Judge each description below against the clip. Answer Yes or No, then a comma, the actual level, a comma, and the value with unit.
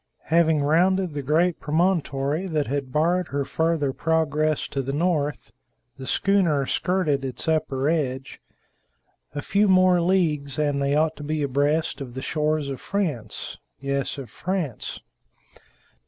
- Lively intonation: No, average, 3.3 semitones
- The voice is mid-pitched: Yes, medium, 150 Hz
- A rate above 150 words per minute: No, average, 140 wpm